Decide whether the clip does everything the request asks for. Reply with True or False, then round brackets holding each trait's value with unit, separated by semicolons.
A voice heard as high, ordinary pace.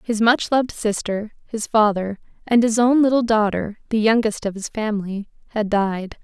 True (215 Hz; 175 wpm)